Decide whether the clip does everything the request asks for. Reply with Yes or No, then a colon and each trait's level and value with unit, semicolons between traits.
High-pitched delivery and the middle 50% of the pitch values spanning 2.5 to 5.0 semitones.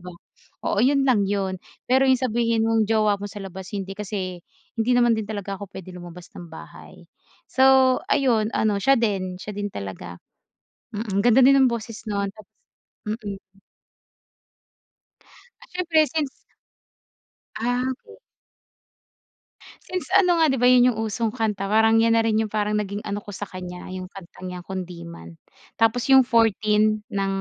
Yes: high, 215 Hz; average, 3.8 semitones